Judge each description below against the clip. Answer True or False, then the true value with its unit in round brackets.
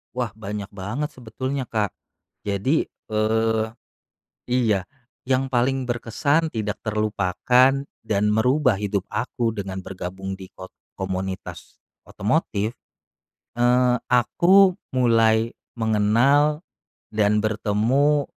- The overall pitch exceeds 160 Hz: False (110 Hz)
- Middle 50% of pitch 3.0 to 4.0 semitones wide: True (3.7 semitones)